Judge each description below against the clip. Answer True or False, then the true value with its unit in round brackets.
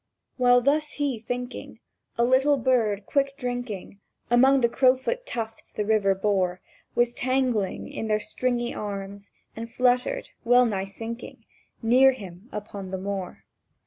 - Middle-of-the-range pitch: False (235 Hz)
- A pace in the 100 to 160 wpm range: True (140 wpm)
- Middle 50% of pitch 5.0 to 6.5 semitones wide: False (3.9 semitones)